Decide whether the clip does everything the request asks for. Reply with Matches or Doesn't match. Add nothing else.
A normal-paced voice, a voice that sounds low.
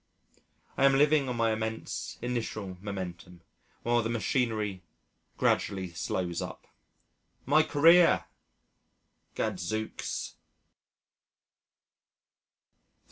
Doesn't match